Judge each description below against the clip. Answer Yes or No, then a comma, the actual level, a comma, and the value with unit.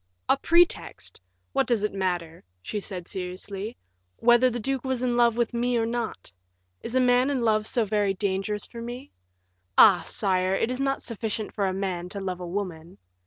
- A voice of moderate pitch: No, high, 215 Hz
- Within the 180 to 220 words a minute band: Yes, average, 190 wpm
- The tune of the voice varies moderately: Yes, average, 4.2 semitones